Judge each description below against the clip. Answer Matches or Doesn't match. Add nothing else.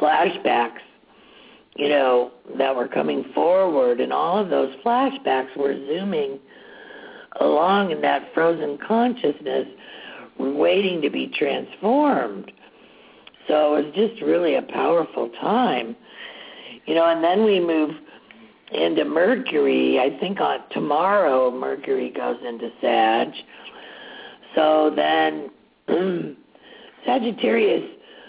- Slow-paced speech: Matches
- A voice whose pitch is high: Doesn't match